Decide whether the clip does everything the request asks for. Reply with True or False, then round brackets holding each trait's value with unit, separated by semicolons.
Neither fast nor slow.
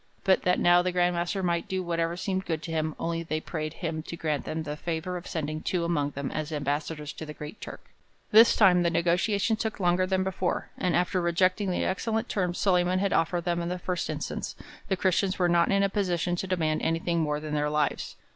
False (225 wpm)